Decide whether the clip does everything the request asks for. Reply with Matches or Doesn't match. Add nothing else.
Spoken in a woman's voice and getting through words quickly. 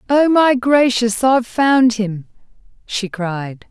Doesn't match